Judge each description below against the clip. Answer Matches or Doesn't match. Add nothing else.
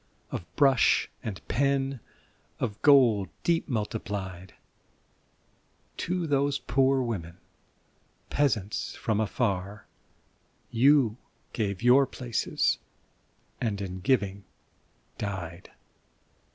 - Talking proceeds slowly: Matches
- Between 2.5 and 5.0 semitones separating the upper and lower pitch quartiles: Doesn't match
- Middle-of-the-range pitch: Doesn't match